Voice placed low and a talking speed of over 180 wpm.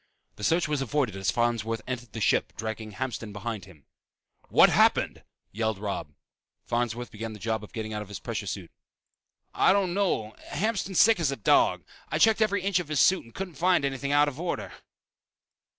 Yes: low, 120 Hz; average, 190 wpm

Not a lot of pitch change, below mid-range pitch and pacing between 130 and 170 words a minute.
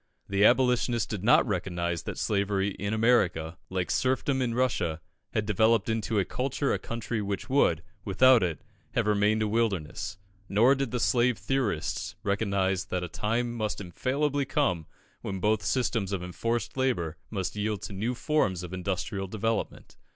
No: average, 4.0 semitones; low, 105 Hz; average, 160 wpm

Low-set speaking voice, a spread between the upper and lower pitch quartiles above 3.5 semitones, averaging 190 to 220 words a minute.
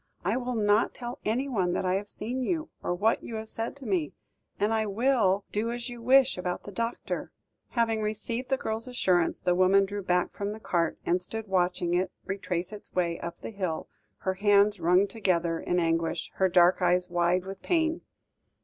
No: high, 200 Hz; average, 4.1 semitones; average, 195 wpm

